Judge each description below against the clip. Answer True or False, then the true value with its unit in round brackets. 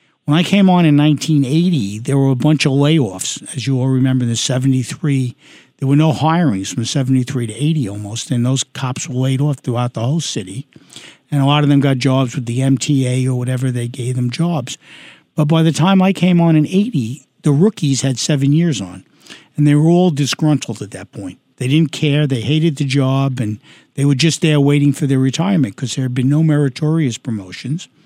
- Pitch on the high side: False (140 Hz)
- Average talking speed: False (215 wpm)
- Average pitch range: True (3.0 semitones)